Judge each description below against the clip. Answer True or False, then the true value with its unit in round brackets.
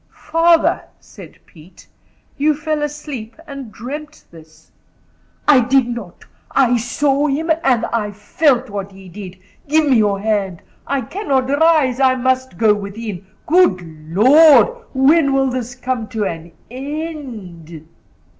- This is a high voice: True (255 Hz)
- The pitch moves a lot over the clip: True (5.8 semitones)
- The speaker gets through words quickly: False (135 wpm)